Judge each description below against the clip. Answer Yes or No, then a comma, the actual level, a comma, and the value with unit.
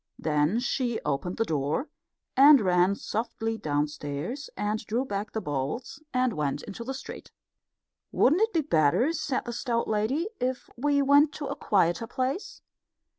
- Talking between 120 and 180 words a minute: Yes, average, 155 wpm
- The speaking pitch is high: Yes, high, 225 Hz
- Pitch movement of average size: No, wide, 7.5 semitones